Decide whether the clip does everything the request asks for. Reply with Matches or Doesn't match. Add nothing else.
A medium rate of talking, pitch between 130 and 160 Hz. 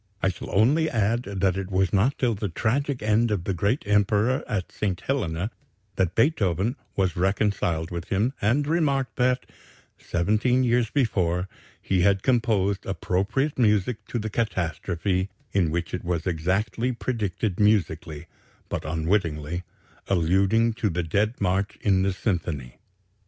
Doesn't match